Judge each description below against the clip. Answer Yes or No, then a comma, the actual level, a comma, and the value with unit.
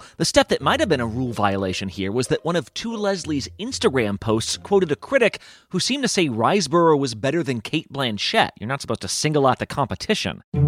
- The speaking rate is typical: No, fast, 220 wpm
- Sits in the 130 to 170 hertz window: Yes, medium, 140 Hz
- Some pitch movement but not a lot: No, wide, 7.8 semitones